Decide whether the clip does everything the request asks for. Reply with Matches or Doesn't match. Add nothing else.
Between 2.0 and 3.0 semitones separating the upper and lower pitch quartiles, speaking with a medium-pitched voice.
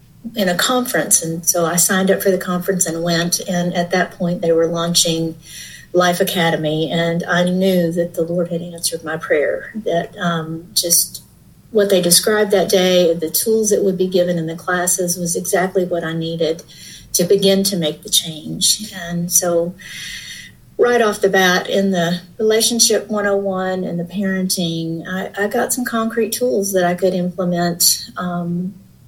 Matches